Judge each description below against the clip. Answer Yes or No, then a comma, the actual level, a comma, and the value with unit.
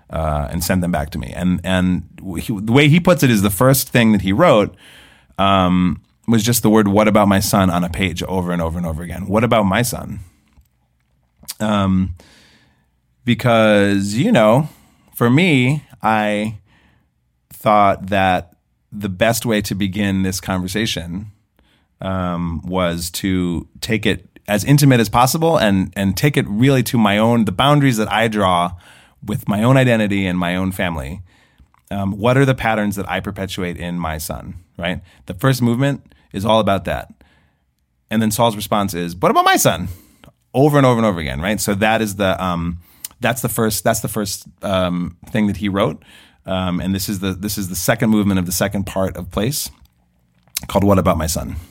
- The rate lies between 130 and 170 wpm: No, average, 190 wpm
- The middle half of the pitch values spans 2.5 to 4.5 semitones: Yes, average, 3.9 semitones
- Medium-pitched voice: No, low, 100 Hz